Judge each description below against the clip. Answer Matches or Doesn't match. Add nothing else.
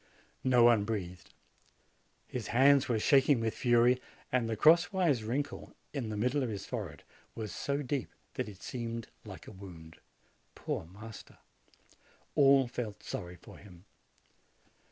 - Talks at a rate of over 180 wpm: Doesn't match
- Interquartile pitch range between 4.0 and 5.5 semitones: Matches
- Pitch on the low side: Matches